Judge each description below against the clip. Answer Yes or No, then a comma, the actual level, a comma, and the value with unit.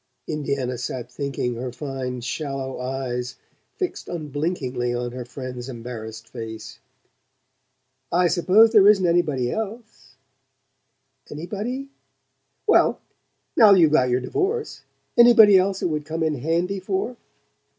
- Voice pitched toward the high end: No, medium, 140 Hz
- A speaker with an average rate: No, slow, 125 wpm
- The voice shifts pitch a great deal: Yes, wide, 6.9 semitones